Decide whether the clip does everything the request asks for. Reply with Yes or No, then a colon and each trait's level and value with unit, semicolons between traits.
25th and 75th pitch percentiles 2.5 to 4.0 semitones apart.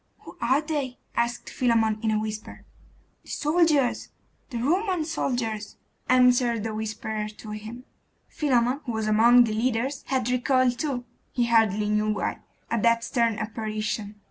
Yes: average, 2.9 semitones